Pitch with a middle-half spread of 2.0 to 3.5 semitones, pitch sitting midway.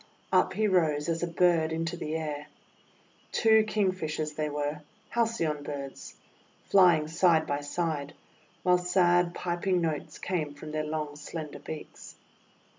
Yes: average, 2.9 semitones; medium, 160 Hz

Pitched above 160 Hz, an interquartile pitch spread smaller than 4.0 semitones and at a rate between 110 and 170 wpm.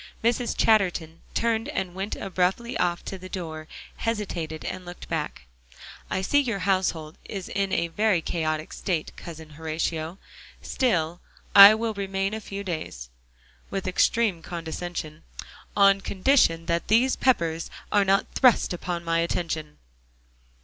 Yes: medium, 185 Hz; average, 3.6 semitones; slow, 135 wpm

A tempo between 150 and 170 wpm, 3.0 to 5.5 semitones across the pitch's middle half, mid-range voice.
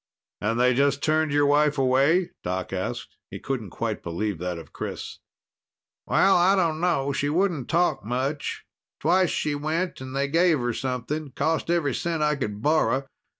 Yes: average, 165 wpm; average, 4.2 semitones; medium, 145 Hz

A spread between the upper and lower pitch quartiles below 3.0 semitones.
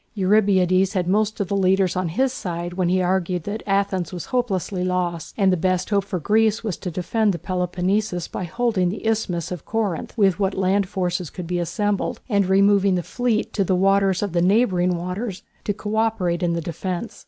Yes: narrow, 2.4 semitones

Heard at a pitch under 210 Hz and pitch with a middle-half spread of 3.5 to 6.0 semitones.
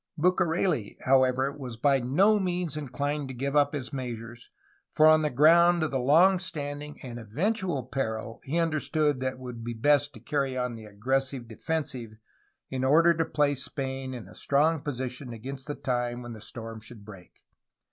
Yes: low, 135 Hz; average, 3.8 semitones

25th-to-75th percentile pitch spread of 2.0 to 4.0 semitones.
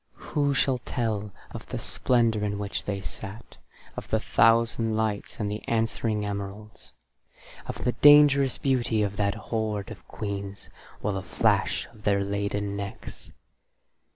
Yes: narrow, 2.4 semitones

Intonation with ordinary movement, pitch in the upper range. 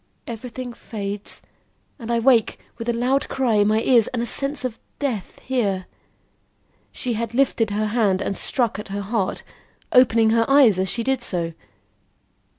Yes: average, 3.2 semitones; high, 230 Hz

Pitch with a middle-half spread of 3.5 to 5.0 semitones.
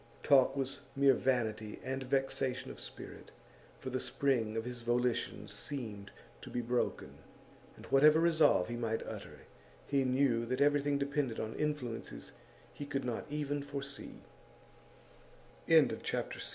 No: average, 2.9 semitones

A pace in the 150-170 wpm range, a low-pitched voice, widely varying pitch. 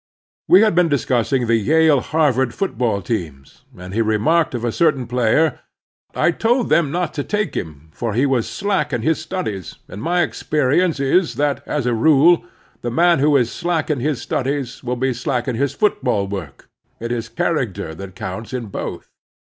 No: average, 185 wpm; low, 130 Hz; wide, 5.9 semitones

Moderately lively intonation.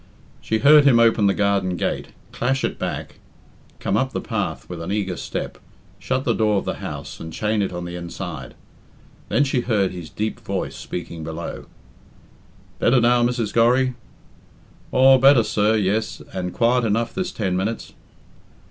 Yes: average, 4.8 semitones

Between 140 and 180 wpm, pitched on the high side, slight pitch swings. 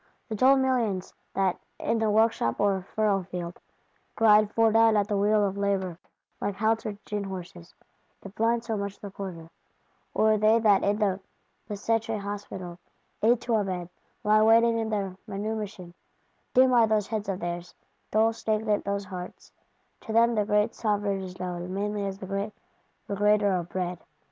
Yes: average, 165 wpm; high, 205 Hz; narrow, 2.3 semitones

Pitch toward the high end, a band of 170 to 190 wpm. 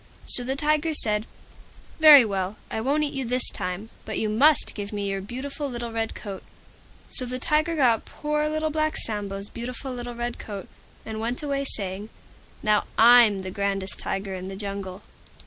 Yes: high, 230 Hz; average, 180 wpm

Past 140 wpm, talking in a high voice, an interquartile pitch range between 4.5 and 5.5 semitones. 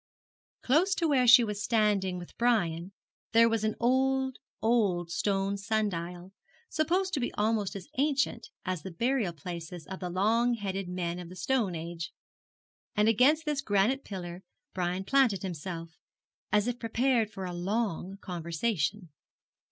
Yes: average, 150 wpm; high, 205 Hz; average, 5.1 semitones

